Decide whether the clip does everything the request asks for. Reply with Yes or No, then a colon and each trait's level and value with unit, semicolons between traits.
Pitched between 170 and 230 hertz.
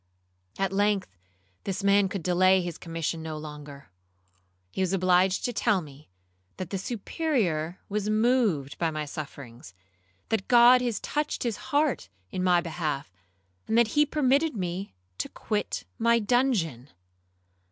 Yes: high, 190 Hz